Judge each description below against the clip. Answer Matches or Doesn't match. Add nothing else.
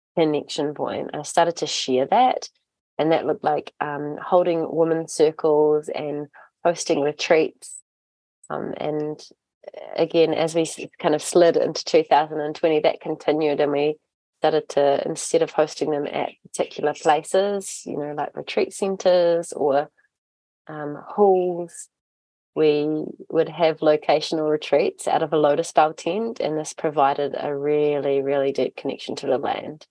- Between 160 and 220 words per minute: Doesn't match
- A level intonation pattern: Matches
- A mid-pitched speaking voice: Matches